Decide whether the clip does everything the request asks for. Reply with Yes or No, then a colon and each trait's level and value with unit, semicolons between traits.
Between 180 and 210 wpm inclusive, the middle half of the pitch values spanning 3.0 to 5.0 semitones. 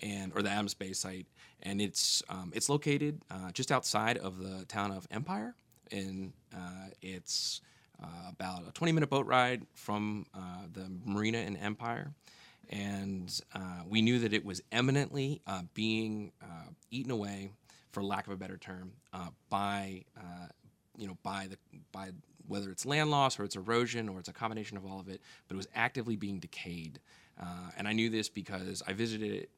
Yes: average, 185 wpm; average, 3.3 semitones